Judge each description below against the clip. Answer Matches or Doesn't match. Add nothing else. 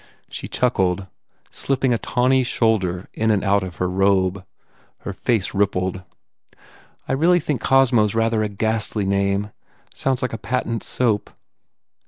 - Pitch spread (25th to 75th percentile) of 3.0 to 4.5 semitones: Matches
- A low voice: Matches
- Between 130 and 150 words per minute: Matches